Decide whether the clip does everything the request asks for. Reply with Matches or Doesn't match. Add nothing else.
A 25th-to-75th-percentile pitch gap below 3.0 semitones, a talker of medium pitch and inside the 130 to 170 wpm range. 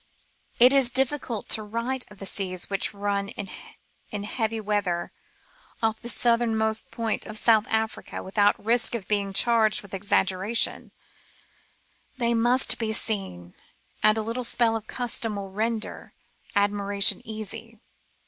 Doesn't match